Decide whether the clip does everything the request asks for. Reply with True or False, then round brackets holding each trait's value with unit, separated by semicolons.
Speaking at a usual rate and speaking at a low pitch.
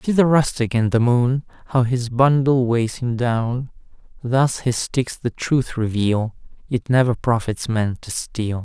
True (165 wpm; 120 Hz)